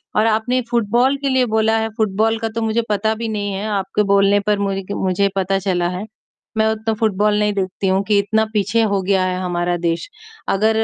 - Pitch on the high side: Yes, high, 210 Hz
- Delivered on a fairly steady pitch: Yes, narrow, 2.3 semitones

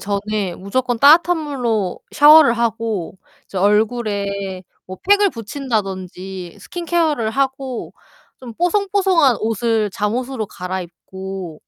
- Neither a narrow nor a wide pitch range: No, wide, 6.0 semitones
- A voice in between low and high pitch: No, high, 225 Hz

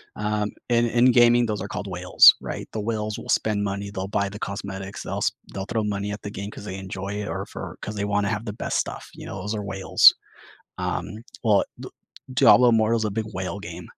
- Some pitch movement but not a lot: No, narrow, 1.8 semitones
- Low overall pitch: Yes, low, 105 Hz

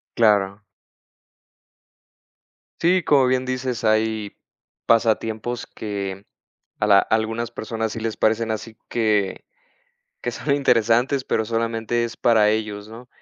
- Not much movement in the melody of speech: Yes, narrow, 1.8 semitones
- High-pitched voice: No, low, 110 Hz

